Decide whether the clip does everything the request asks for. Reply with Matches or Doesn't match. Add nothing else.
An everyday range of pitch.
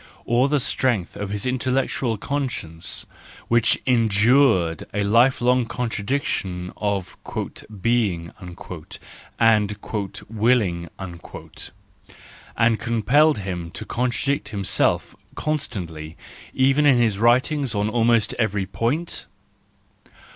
Matches